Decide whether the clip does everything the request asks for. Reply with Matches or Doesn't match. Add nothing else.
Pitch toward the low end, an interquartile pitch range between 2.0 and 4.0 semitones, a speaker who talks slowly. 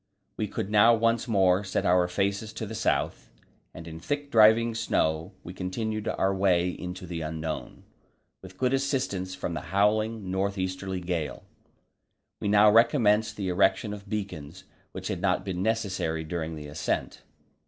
Doesn't match